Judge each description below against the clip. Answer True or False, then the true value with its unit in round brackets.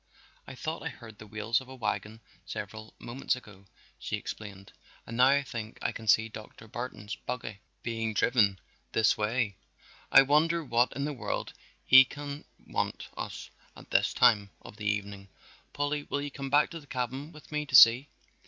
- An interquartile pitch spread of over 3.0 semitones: True (4.4 semitones)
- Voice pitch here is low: True (120 Hz)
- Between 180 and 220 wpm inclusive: True (185 wpm)